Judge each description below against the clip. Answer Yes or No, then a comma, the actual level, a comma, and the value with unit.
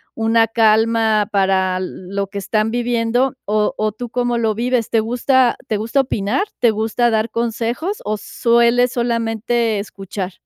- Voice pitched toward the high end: Yes, high, 225 Hz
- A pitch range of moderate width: No, narrow, 2.0 semitones